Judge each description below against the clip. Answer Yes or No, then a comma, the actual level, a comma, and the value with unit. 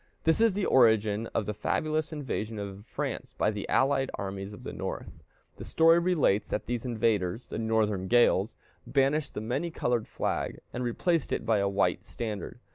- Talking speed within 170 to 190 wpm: Yes, average, 180 wpm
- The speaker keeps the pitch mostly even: No, average, 5.3 semitones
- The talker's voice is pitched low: Yes, low, 115 Hz